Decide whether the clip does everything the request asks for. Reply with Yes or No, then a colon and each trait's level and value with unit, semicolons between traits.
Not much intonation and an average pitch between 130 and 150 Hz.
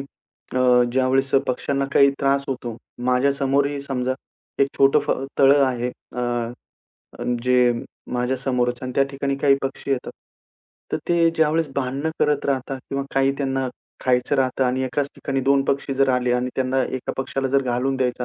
Yes: narrow, 1.5 semitones; low, 135 Hz